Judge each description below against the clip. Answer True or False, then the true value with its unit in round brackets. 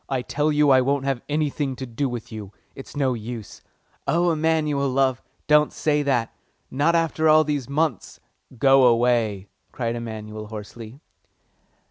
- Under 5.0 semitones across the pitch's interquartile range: True (4.2 semitones)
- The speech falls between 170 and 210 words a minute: False (155 wpm)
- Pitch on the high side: False (135 Hz)